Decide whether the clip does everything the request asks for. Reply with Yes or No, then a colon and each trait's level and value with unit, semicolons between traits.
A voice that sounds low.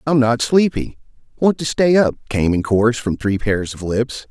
Yes: low, 120 Hz